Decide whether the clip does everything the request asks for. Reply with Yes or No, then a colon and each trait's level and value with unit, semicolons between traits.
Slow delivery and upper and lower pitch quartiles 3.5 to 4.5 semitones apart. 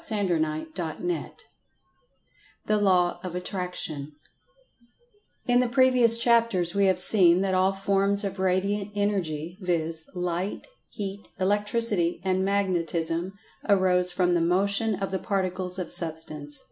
No: slow, 130 wpm; narrow, 2.5 semitones